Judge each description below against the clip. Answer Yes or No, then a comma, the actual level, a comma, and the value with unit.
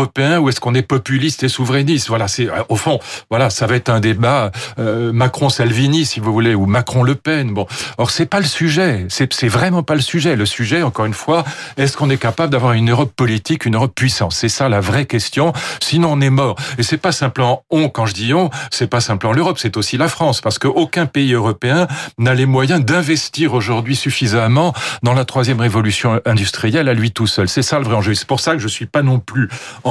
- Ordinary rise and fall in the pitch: Yes, average, 4.3 semitones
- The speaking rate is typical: No, fast, 230 wpm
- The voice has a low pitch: Yes, low, 130 Hz